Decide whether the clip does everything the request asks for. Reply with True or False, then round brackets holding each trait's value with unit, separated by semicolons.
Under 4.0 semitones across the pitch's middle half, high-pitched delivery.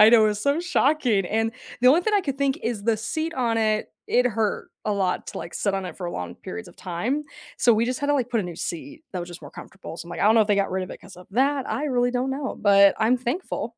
False (5.2 semitones; 225 Hz)